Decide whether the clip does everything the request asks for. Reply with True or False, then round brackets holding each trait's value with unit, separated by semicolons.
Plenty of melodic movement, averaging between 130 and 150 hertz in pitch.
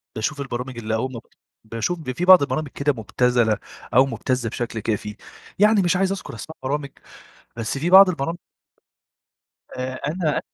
True (5.9 semitones; 135 Hz)